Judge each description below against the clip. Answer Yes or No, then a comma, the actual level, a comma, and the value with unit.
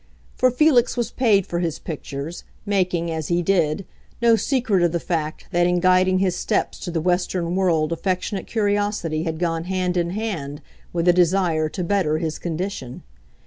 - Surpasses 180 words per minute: No, average, 175 wpm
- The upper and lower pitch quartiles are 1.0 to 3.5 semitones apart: Yes, average, 3.1 semitones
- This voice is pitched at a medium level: Yes, medium, 180 Hz